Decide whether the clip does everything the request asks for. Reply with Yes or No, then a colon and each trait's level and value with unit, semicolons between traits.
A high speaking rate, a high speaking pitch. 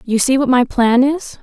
Yes: fast, 250 wpm; very high, 255 Hz